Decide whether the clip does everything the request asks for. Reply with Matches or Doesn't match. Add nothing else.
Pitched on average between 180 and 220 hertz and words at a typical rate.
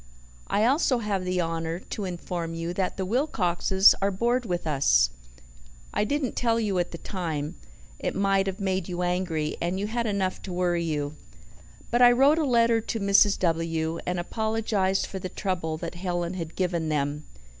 Matches